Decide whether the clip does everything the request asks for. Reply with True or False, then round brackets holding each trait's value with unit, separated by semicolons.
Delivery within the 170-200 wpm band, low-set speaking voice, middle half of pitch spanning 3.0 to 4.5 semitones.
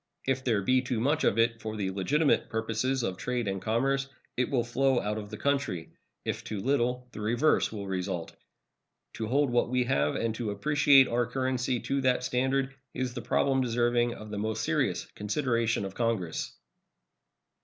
True (180 wpm; 120 Hz; 3.4 semitones)